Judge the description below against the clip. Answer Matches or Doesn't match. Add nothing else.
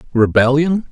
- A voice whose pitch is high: Doesn't match